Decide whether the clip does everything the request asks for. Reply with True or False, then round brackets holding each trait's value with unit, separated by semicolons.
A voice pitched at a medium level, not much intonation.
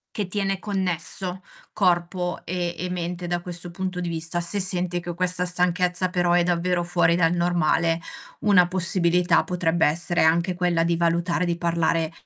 True (175 Hz; 1.0 semitones)